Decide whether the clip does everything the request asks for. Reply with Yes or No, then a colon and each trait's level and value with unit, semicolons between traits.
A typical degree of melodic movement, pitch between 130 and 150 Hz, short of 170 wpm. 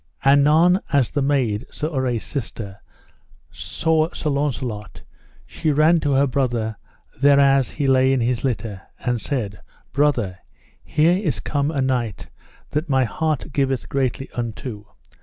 Yes: average, 3.6 semitones; low, 135 Hz; average, 140 wpm